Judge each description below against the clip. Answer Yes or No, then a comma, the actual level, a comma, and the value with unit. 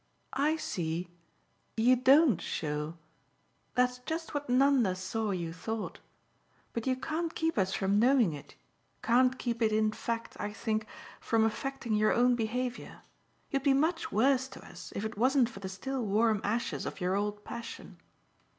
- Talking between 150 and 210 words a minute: Yes, average, 160 wpm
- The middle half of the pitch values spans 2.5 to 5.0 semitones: Yes, average, 4.1 semitones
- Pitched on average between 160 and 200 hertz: No, high, 230 Hz